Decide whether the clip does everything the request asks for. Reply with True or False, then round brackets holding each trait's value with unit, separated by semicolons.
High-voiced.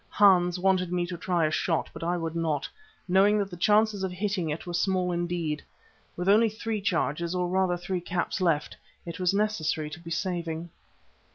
False (180 Hz)